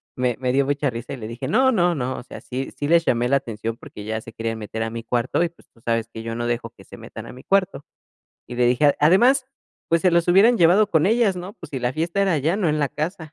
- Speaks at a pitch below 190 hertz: Yes, medium, 140 Hz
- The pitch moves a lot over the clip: Yes, wide, 6.7 semitones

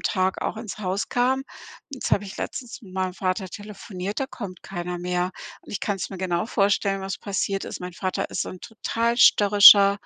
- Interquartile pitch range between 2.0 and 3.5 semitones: Yes, narrow, 2.4 semitones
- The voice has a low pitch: No, high, 195 Hz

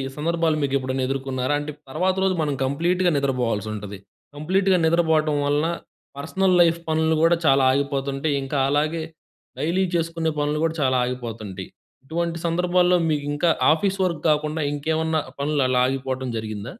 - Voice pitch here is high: No, medium, 150 Hz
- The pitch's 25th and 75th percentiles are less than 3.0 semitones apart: No, average, 3.7 semitones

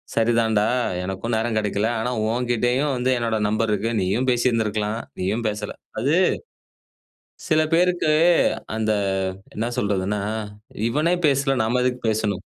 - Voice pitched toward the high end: No, low, 115 Hz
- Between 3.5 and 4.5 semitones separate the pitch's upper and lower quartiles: No, average, 2.9 semitones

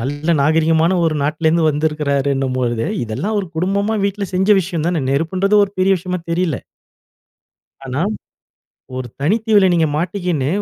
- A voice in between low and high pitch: Yes, medium, 165 Hz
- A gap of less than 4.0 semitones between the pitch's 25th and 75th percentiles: No, average, 4.4 semitones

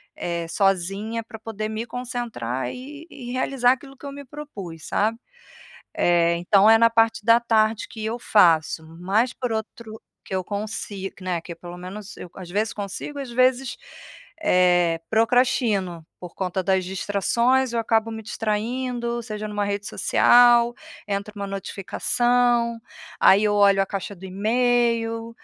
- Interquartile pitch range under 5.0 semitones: Yes, average, 3.6 semitones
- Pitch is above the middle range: Yes, high, 215 Hz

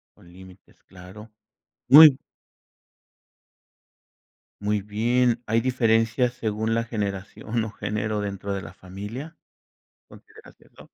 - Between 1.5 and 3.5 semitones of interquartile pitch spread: Yes, average, 3.1 semitones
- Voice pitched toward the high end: No, low, 110 Hz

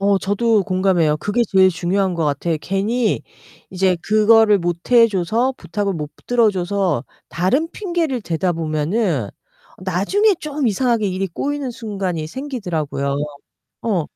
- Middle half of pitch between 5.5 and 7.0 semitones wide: No, average, 5.1 semitones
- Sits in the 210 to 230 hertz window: No, high, 195 Hz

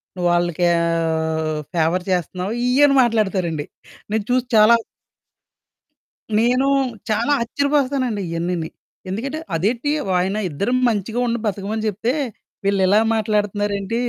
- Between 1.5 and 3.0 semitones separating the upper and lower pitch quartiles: No, average, 5.0 semitones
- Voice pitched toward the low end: No, high, 205 Hz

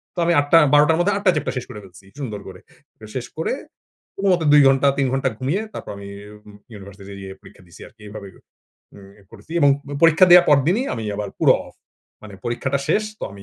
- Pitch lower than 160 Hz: Yes, low, 135 Hz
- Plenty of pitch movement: Yes, wide, 7.8 semitones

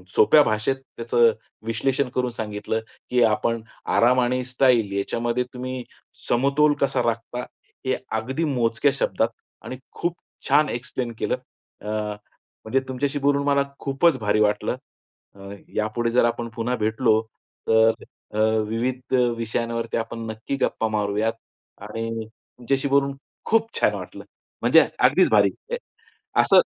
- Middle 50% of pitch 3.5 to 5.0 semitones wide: No, average, 3.0 semitones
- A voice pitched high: No, low, 120 Hz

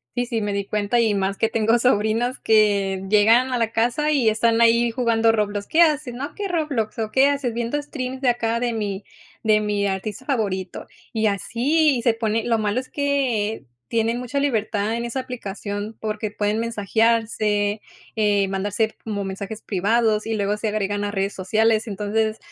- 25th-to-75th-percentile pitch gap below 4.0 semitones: Yes, narrow, 2.5 semitones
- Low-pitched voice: No, high, 220 Hz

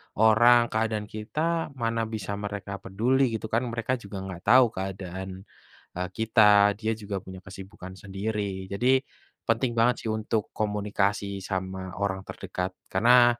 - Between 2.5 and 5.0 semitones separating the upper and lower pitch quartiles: Yes, average, 3.0 semitones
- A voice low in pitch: Yes, low, 105 Hz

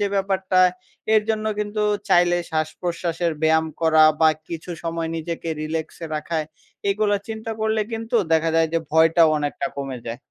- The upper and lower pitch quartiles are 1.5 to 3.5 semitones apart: No, average, 3.9 semitones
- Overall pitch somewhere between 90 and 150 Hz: No, medium, 165 Hz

